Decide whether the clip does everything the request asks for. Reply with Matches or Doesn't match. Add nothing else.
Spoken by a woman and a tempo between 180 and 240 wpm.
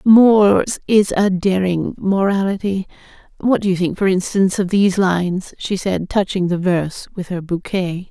Doesn't match